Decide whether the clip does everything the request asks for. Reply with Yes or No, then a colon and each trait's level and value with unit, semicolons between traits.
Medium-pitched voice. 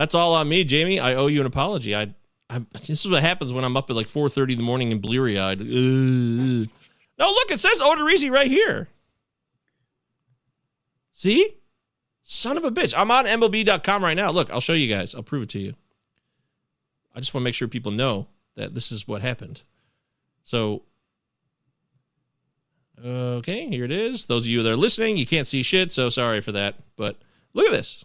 No: low, 130 Hz